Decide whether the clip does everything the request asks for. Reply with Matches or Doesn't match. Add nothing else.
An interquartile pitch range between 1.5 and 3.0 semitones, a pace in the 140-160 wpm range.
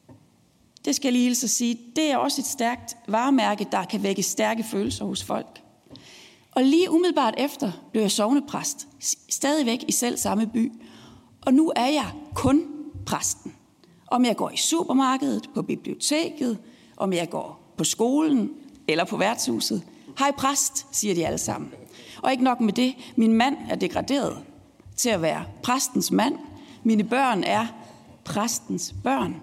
Doesn't match